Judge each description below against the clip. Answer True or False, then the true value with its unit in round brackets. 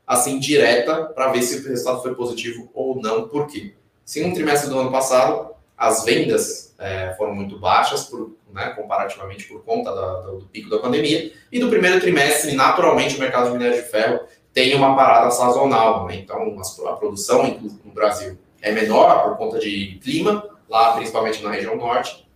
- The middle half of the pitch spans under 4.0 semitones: False (5.0 semitones)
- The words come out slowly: False (185 wpm)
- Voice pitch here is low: True (120 Hz)